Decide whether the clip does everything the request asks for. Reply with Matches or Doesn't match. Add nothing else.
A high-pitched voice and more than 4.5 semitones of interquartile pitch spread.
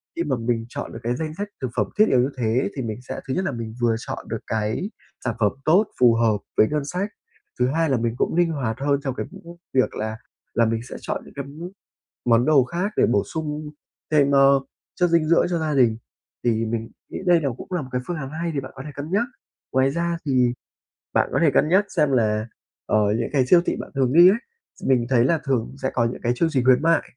Doesn't match